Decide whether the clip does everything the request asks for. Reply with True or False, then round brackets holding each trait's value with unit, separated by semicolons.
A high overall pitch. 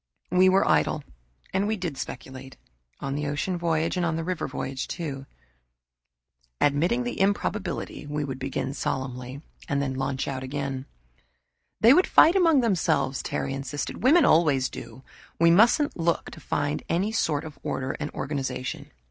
False (150 Hz)